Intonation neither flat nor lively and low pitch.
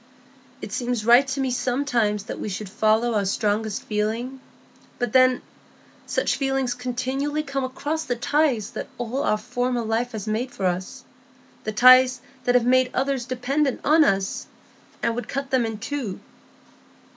No: average, 3.2 semitones; high, 245 Hz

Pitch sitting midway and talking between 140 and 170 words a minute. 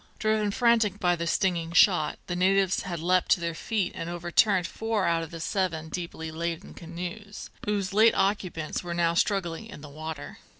No: medium, 175 Hz; average, 180 wpm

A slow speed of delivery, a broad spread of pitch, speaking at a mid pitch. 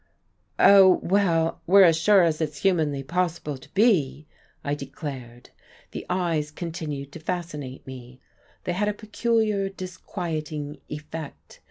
No: slow, 130 wpm; average, 4.2 semitones; medium, 160 Hz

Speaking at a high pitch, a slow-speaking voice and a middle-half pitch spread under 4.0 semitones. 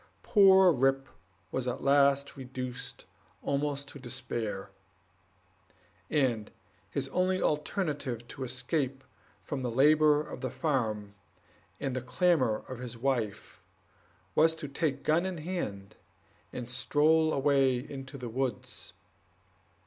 No: low, 135 Hz; slow, 115 wpm; average, 3.3 semitones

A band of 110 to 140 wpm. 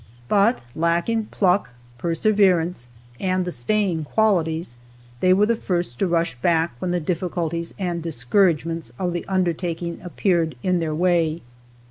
Yes: slow, 135 wpm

